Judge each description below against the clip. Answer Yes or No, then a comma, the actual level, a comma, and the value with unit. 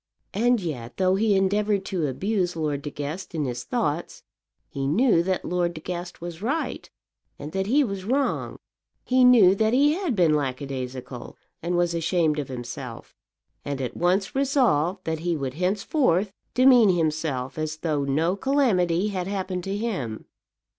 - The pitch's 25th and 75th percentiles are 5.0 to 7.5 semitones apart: Yes, average, 5.3 semitones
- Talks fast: No, average, 160 wpm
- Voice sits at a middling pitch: Yes, medium, 180 Hz